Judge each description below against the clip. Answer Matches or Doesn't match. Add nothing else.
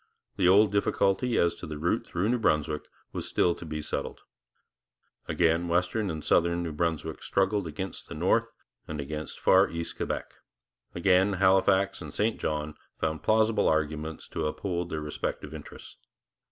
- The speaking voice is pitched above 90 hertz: Doesn't match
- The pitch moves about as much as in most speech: Matches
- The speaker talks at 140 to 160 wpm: Matches